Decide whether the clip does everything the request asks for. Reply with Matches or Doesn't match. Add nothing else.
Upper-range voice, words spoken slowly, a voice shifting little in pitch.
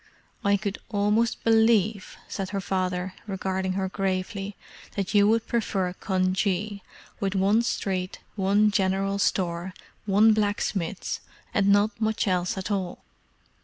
Matches